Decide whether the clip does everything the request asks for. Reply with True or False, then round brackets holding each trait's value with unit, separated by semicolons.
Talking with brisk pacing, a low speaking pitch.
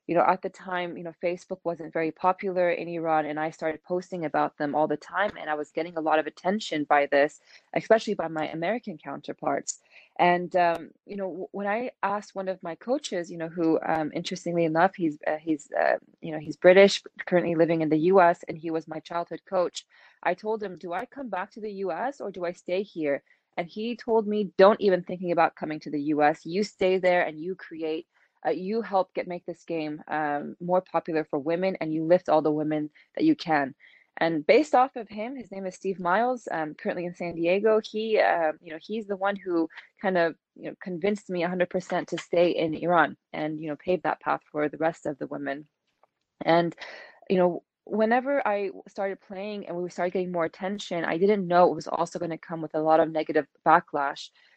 False (220 wpm; 175 Hz)